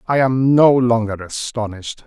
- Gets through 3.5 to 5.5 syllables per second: Yes, 4.7 syllables/s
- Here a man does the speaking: Yes, male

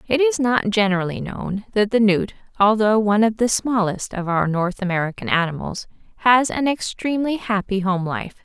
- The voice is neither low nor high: No, high, 210 Hz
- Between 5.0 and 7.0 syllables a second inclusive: Yes, 5.2 syllables/s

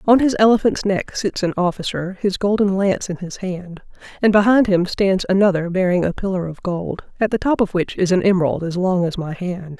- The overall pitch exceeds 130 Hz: Yes, medium, 185 Hz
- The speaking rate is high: Yes, fast, 220 wpm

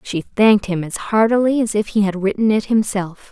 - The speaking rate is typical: No, fast, 215 wpm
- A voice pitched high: Yes, high, 205 Hz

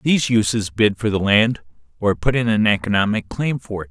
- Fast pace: Yes, fast, 215 wpm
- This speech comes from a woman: No, male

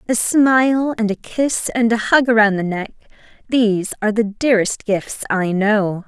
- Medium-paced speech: Yes, average, 180 wpm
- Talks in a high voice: Yes, high, 220 Hz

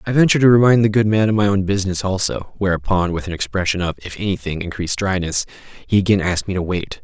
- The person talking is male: Yes, male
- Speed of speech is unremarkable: No, fast, 230 wpm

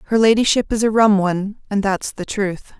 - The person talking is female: Yes, female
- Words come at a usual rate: No, fast, 215 wpm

